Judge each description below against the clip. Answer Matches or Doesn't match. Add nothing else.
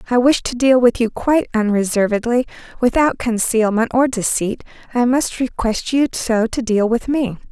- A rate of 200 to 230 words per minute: Doesn't match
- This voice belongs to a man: Doesn't match